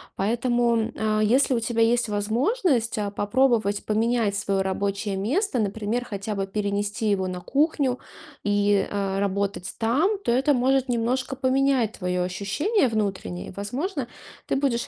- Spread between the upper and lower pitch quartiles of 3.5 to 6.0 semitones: Yes, average, 4.1 semitones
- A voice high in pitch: Yes, high, 225 Hz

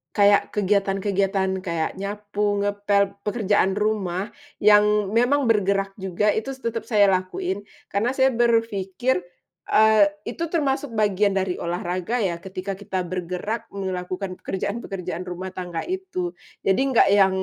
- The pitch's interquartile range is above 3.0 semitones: No, narrow, 2.6 semitones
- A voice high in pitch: Yes, high, 200 Hz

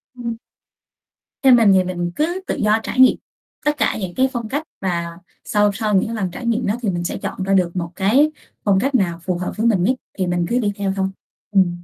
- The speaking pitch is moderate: No, high, 200 Hz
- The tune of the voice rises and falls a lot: No, average, 4.5 semitones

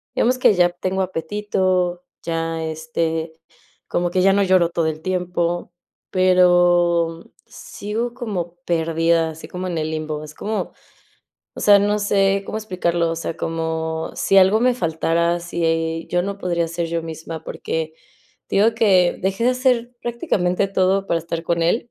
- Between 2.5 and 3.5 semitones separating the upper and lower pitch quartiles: Yes, average, 3.0 semitones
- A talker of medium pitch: Yes, medium, 175 Hz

